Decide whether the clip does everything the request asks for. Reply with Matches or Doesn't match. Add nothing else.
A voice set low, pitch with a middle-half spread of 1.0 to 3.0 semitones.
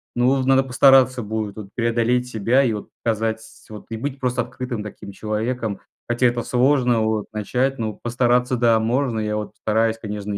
Matches